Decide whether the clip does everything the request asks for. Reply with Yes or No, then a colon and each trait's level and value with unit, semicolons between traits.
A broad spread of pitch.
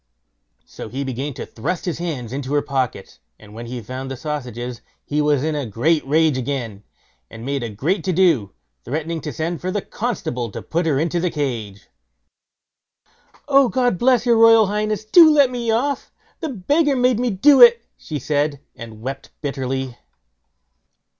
Yes: wide, 8.9 semitones